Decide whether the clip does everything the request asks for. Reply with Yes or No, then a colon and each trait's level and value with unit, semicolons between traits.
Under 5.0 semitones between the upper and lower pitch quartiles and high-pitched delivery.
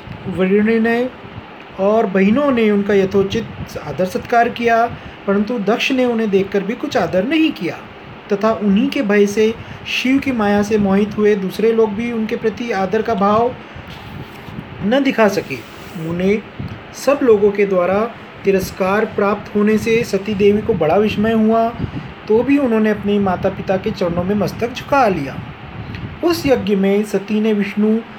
Yes: narrow, 2.4 semitones; high, 215 Hz